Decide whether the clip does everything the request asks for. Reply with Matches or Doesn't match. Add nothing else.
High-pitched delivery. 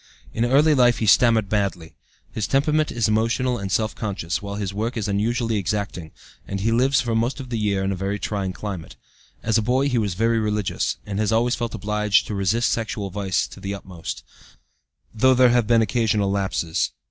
Doesn't match